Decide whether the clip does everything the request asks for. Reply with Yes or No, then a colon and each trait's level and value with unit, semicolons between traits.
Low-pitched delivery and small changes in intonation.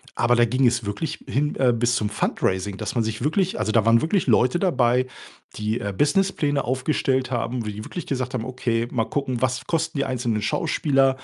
No: low, 125 Hz; average, 3.2 semitones